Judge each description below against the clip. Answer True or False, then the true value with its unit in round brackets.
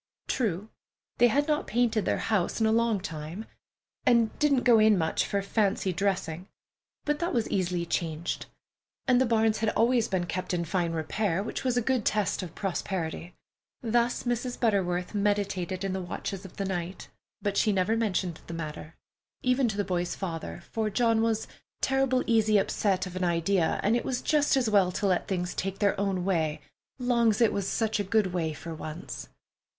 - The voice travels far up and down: False (4.2 semitones)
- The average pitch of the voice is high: True (200 Hz)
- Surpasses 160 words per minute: True (185 wpm)